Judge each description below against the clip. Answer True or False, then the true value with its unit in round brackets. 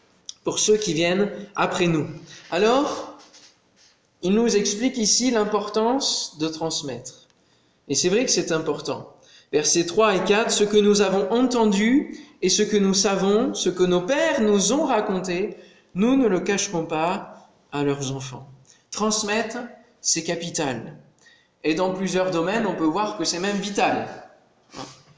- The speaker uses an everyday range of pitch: True (4.6 semitones)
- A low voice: False (200 Hz)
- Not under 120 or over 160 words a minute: True (150 wpm)